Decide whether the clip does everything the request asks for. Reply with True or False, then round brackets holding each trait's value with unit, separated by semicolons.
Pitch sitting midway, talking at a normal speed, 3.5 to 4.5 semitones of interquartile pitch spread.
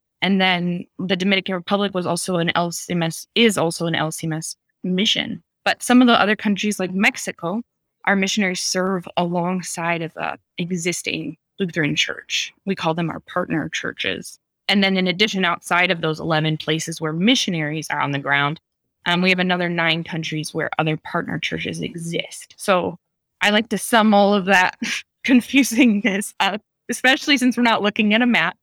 True (180 Hz; 170 wpm; 3.9 semitones)